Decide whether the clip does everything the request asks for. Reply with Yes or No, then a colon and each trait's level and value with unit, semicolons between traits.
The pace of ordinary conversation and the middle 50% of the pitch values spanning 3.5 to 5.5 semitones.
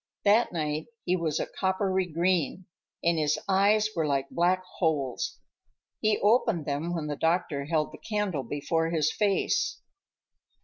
Yes: average, 145 wpm; average, 4.0 semitones